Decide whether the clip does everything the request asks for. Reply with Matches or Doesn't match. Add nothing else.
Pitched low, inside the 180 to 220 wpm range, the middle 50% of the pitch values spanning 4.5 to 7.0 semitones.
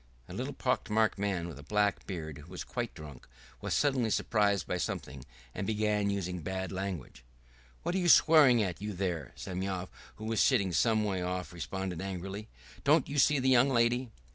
Doesn't match